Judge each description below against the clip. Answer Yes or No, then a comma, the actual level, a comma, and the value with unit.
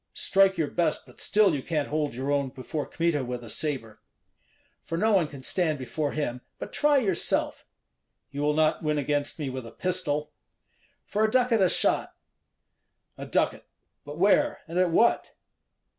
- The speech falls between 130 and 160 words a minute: No, average, 175 wpm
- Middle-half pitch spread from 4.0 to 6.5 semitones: Yes, average, 4.5 semitones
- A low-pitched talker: No, medium, 155 Hz